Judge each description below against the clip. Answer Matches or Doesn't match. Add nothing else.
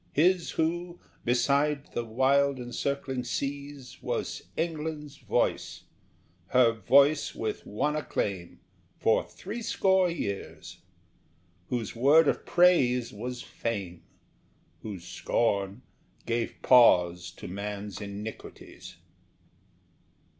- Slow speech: Matches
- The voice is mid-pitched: Doesn't match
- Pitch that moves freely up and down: Matches